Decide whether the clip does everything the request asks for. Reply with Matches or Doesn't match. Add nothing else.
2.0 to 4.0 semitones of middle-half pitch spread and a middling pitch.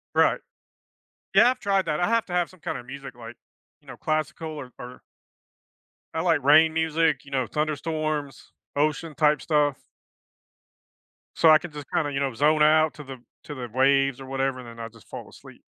Matches